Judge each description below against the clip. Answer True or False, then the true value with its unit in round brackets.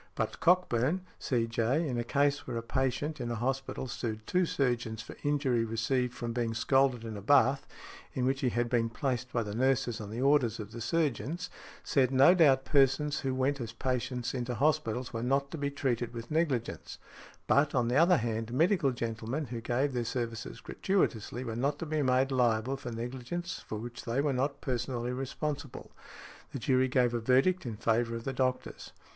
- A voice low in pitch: True (125 Hz)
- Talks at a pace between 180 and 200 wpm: True (190 wpm)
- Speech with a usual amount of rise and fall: True (3.0 semitones)